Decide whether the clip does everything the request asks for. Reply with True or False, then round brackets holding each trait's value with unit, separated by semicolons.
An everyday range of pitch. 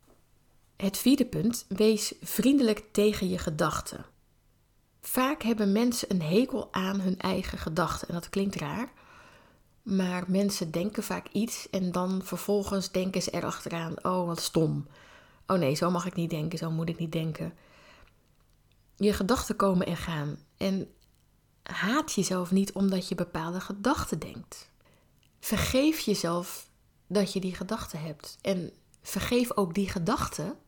True (3.2 semitones)